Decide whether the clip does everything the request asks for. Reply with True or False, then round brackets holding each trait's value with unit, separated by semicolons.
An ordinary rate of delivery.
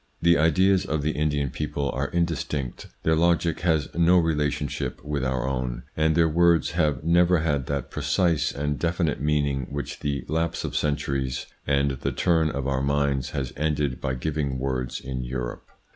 True (175 wpm)